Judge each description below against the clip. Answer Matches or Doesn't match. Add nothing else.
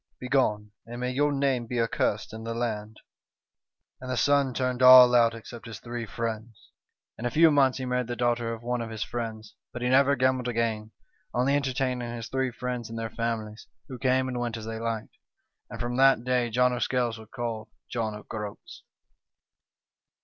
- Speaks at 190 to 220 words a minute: Matches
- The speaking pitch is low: Matches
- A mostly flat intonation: Matches